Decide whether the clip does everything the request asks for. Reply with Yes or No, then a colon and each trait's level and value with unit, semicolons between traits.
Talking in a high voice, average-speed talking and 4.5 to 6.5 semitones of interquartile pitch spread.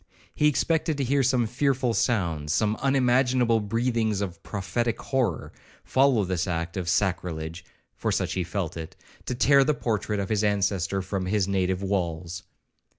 No: low, 105 Hz; average, 155 wpm; average, 5.3 semitones